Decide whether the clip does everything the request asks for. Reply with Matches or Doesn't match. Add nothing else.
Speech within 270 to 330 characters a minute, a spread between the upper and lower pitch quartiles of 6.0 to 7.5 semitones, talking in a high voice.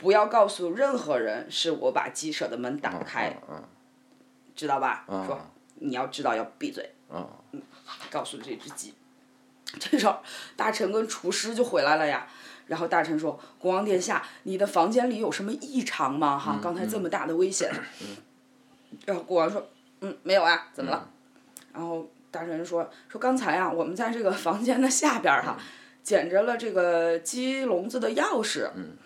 Doesn't match